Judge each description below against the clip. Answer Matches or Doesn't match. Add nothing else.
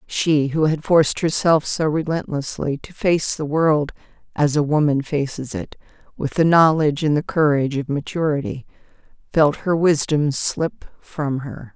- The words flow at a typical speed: Matches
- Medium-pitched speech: Matches